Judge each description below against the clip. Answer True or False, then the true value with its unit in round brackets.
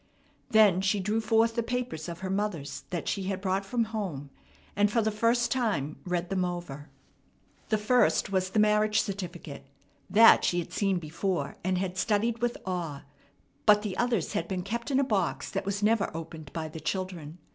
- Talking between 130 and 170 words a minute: False (190 wpm)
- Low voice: False (195 Hz)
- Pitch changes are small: False (3.8 semitones)